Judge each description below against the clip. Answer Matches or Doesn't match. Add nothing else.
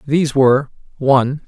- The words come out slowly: Matches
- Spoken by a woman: Doesn't match